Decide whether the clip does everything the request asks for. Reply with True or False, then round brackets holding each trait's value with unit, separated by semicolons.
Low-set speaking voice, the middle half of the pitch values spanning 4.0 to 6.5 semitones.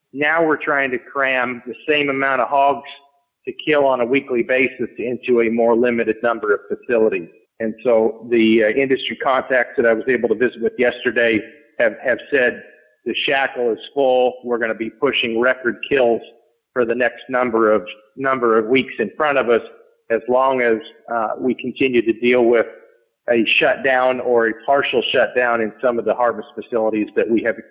False (125 Hz; 2.8 semitones)